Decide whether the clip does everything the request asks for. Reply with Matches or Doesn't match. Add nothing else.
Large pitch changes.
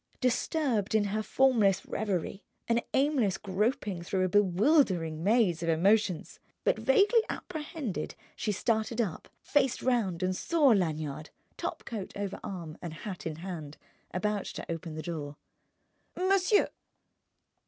Matches